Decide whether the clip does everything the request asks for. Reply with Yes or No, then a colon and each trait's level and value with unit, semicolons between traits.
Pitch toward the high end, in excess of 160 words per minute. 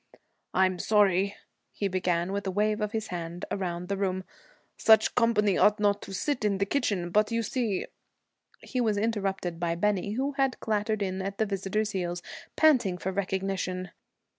Yes: high, 200 Hz; average, 175 wpm